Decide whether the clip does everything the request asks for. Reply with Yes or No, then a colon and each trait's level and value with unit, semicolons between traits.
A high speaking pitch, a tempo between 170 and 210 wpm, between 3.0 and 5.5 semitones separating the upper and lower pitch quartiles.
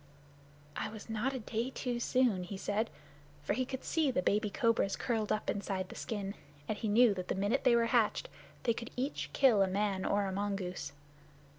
Yes: high, 215 Hz; average, 200 wpm; average, 3.3 semitones